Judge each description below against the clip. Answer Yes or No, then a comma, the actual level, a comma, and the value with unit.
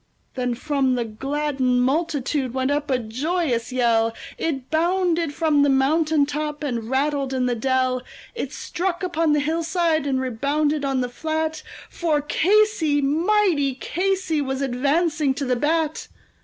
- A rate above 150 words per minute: No, average, 145 wpm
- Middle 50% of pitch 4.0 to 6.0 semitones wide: No, average, 3.6 semitones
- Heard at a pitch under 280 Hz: No, very high, 290 Hz